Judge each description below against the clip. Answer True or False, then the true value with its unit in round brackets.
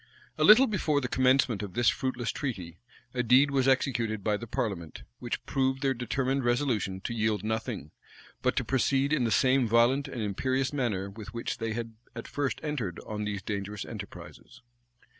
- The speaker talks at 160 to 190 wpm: True (180 wpm)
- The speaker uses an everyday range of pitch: True (3.9 semitones)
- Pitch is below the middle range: True (120 Hz)